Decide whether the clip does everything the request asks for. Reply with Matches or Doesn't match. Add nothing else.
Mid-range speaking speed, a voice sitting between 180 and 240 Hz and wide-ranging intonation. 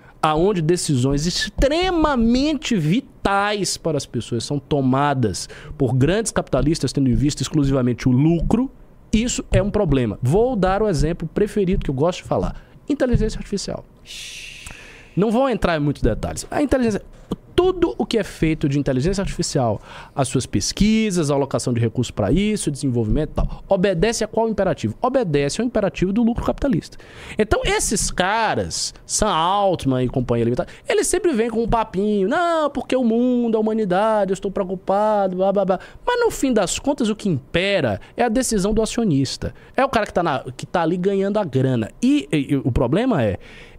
Matches